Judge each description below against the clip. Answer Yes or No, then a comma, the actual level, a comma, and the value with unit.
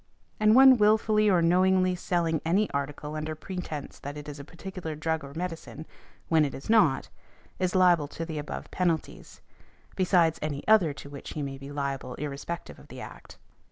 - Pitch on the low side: No, medium, 160 Hz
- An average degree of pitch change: Yes, average, 4.0 semitones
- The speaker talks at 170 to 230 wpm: Yes, average, 180 wpm